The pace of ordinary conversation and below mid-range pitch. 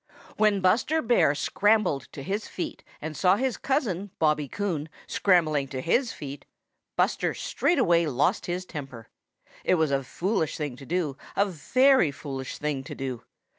No: average, 155 wpm; medium, 165 Hz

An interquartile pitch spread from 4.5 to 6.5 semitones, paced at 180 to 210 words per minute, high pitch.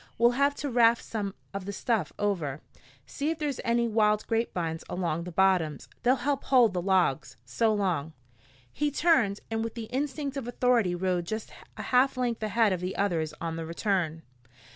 Yes: wide, 5.5 semitones; average, 185 wpm; high, 210 Hz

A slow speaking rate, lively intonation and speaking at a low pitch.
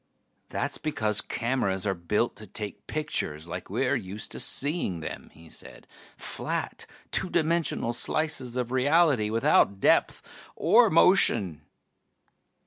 Yes: slow, 125 wpm; wide, 6.7 semitones; low, 115 Hz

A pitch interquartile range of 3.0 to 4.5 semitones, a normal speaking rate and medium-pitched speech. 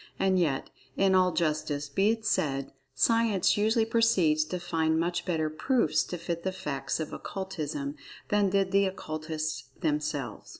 Yes: average, 4.0 semitones; average, 155 wpm; medium, 170 Hz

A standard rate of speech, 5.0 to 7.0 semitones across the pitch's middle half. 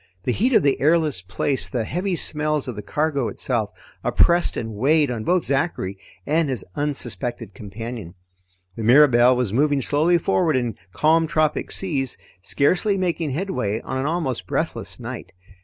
Yes: average, 155 wpm; wide, 5.4 semitones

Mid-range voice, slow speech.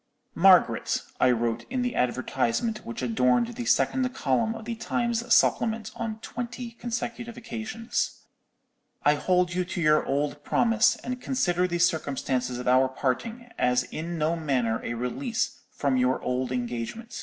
No: medium, 175 Hz; average, 150 wpm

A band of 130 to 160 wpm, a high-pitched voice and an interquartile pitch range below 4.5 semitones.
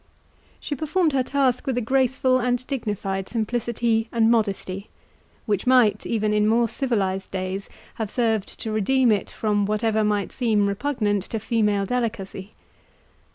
Yes: average, 145 wpm; high, 220 Hz; average, 3.2 semitones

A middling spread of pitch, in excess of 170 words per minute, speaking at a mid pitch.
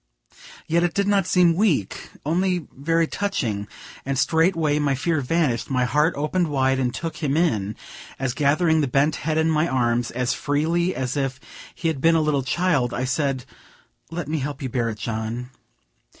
Yes: average, 4.2 semitones; average, 180 wpm; medium, 145 Hz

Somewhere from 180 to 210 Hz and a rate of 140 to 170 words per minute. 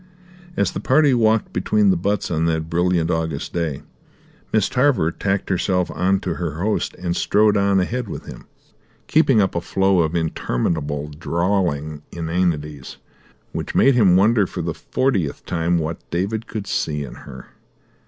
No: very low, 90 Hz; average, 160 wpm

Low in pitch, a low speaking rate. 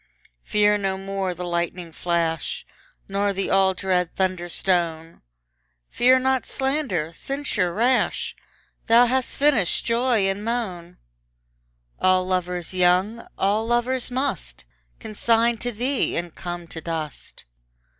No: high, 195 Hz; slow, 120 wpm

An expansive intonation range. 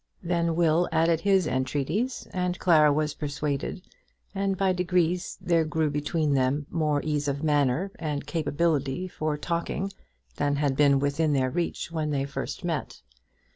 No: average, 3.1 semitones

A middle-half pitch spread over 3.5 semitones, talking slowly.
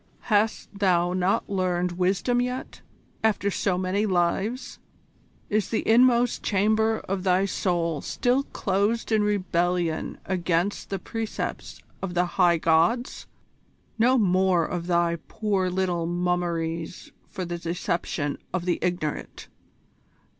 No: average, 3.2 semitones; slow, 120 wpm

